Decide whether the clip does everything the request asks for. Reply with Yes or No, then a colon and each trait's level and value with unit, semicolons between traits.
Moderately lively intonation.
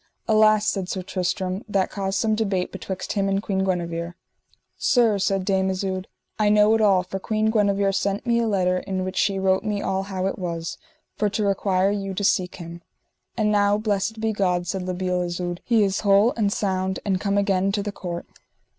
No: narrow, 1.9 semitones